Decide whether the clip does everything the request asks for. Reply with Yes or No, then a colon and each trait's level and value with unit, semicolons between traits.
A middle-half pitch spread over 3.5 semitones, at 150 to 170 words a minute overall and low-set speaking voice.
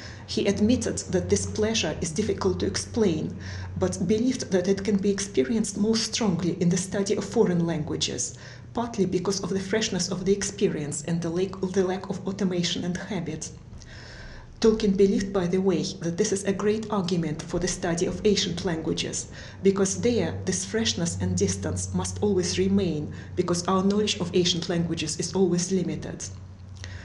No: average, 4.4 semitones; average, 165 wpm; medium, 185 Hz